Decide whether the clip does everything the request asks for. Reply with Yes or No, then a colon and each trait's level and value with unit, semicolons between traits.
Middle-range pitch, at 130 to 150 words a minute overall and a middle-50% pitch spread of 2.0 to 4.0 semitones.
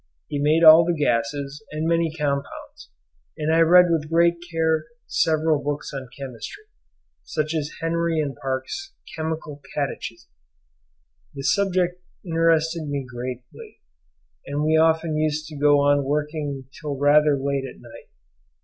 Yes: medium, 150 Hz; average, 140 wpm; narrow, 2.5 semitones